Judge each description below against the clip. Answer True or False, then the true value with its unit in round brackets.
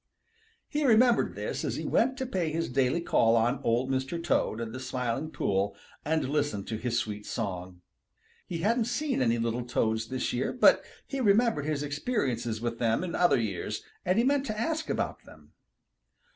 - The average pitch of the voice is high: False (135 Hz)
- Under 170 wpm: False (185 wpm)